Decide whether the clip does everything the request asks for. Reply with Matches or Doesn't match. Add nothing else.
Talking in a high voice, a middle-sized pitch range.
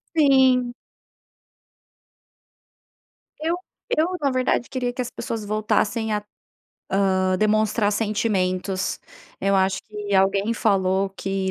Matches